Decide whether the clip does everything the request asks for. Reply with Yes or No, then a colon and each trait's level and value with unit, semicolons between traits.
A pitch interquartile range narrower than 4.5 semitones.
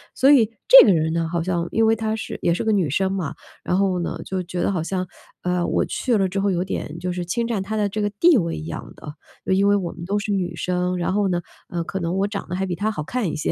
Yes: average, 2.9 semitones